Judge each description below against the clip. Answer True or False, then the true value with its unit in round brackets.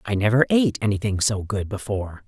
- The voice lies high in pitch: False (105 Hz)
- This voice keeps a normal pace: True (185 wpm)